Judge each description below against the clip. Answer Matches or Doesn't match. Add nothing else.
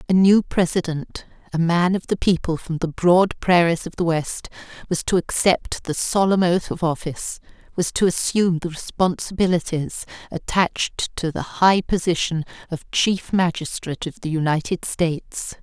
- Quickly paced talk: Doesn't match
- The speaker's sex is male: Doesn't match